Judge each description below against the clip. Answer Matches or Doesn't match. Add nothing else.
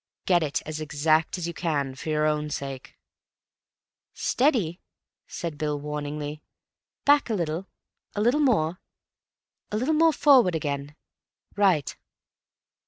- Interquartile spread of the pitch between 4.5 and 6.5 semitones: Matches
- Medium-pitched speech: Matches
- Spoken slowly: Matches